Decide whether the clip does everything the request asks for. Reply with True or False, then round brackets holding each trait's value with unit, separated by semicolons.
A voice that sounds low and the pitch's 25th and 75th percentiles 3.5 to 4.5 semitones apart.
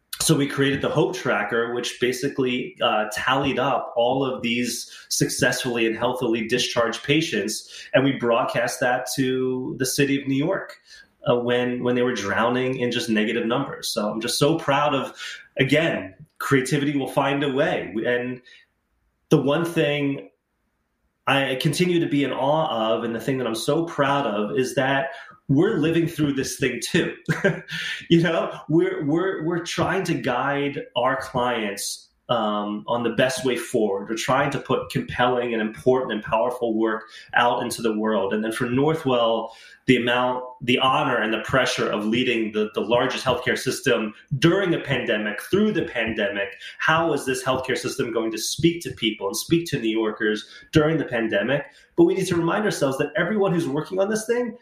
True (130 Hz; 4.2 semitones)